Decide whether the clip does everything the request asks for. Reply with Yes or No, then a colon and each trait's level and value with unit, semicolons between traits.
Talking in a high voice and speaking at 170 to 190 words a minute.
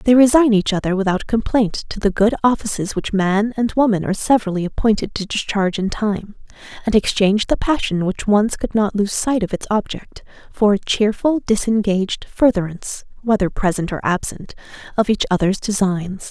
Yes: high, 210 Hz; average, 175 wpm